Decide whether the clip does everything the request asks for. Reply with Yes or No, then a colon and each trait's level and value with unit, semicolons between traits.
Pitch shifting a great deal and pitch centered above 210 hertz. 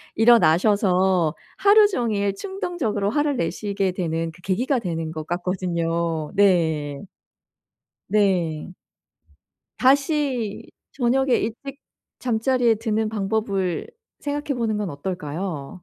No: wide, 5.8 semitones; high, 200 Hz